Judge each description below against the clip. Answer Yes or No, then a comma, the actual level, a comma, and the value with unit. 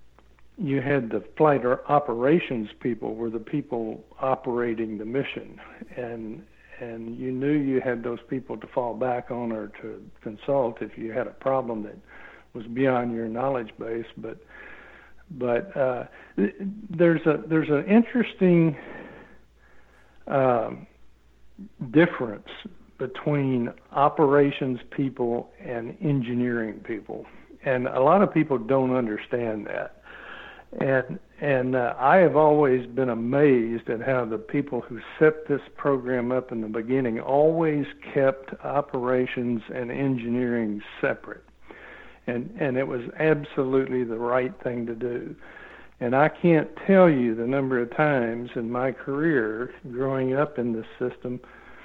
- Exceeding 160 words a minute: No, slow, 135 wpm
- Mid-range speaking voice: No, low, 130 Hz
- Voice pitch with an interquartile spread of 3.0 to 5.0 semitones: Yes, average, 3.3 semitones